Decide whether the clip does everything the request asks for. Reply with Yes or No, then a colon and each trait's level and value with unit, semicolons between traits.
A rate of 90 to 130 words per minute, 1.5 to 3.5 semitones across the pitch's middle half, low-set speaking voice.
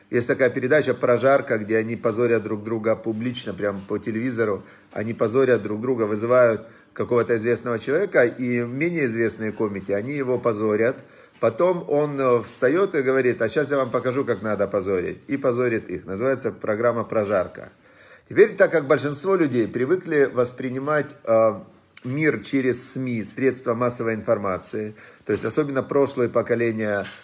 No: average, 145 wpm; average, 3.1 semitones; low, 120 Hz